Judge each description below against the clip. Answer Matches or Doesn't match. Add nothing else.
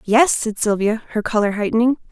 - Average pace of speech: Matches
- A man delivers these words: Doesn't match